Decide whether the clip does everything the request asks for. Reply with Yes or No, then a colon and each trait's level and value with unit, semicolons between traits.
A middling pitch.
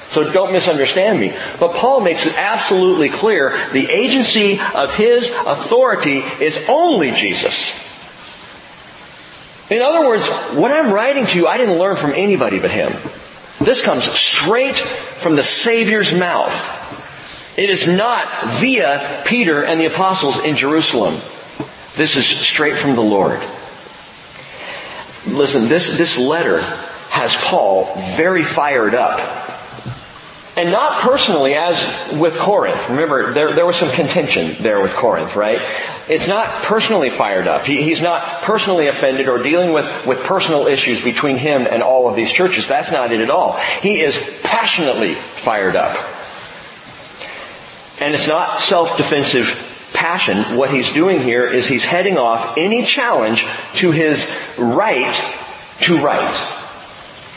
Yes: medium, 175 Hz